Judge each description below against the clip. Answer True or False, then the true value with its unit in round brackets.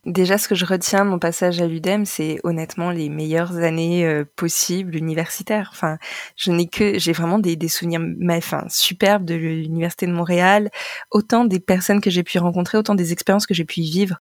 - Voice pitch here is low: False (175 Hz)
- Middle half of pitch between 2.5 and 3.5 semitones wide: True (2.9 semitones)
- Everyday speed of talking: True (205 wpm)